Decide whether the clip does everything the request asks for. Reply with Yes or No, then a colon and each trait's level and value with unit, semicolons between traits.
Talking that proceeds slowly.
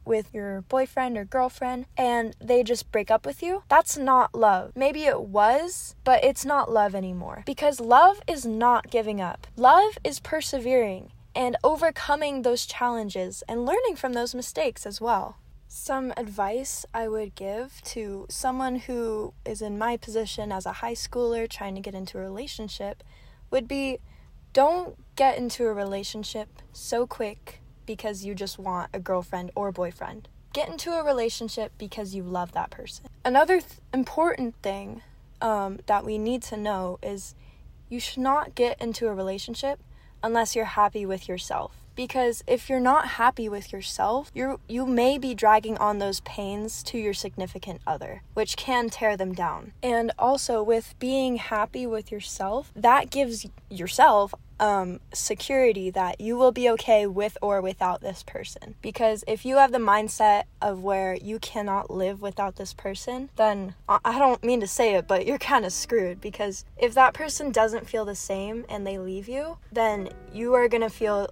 No: average, 170 wpm